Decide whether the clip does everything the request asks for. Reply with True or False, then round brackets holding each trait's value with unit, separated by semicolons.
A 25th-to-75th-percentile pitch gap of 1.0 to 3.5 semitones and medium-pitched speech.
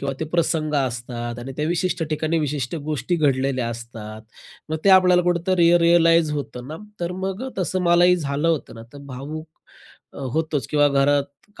False (4.1 semitones; 155 Hz)